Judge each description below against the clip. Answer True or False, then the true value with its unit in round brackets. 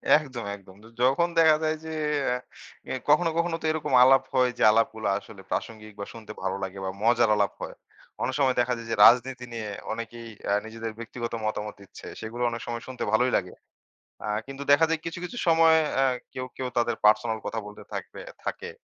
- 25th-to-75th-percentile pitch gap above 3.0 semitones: True (3.7 semitones)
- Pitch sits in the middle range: False (120 Hz)